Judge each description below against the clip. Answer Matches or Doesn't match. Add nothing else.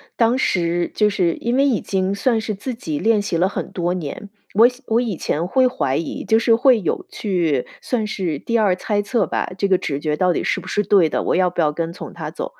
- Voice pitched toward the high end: Matches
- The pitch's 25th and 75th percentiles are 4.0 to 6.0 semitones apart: Matches